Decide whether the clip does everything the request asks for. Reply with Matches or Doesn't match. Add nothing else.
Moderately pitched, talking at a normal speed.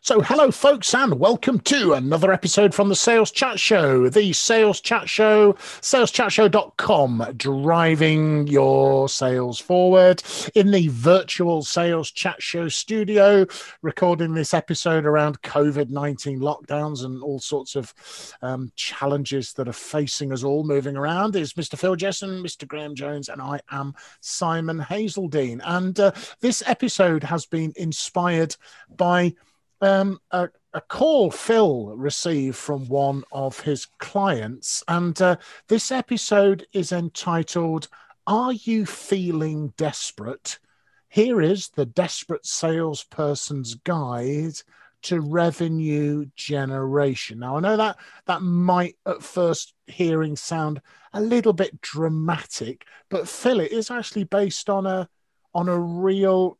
Doesn't match